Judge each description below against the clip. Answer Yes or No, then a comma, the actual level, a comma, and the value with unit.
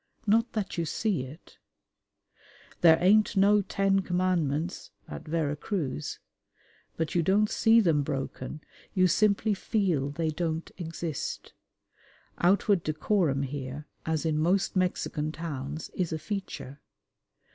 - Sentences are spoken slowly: Yes, slow, 125 wpm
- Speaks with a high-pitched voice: No, medium, 170 Hz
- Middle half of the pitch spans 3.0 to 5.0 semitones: Yes, average, 4.4 semitones